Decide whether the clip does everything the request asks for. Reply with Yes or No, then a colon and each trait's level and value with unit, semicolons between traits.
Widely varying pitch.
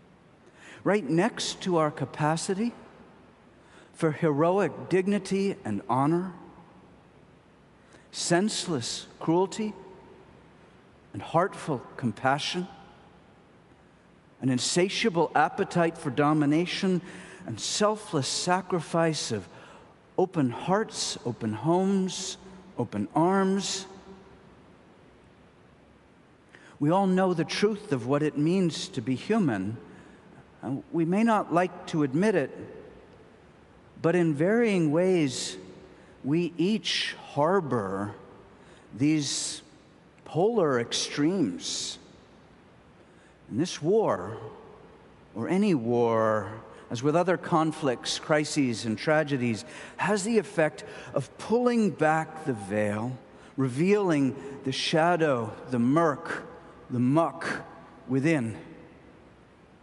Yes: wide, 6.4 semitones